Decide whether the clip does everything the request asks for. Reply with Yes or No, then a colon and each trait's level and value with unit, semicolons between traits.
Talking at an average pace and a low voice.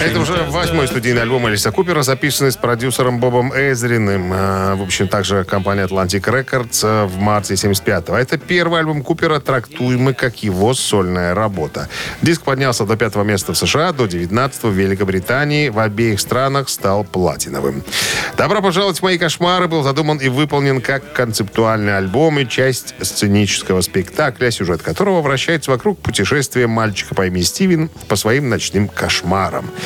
Yes: average, 150 wpm; low, 125 Hz